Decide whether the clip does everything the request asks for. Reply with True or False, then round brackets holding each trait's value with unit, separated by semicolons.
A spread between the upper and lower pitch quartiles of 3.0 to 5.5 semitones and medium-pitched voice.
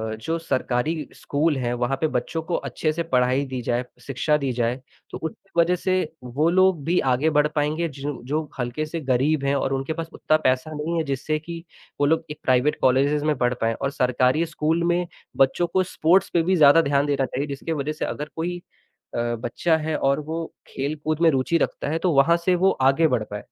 True (3.6 semitones; 150 Hz)